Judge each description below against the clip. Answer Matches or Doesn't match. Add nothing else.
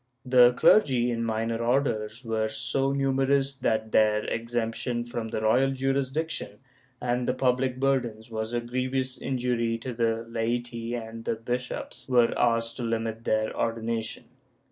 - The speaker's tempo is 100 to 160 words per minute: Matches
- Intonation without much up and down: Matches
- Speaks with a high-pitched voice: Doesn't match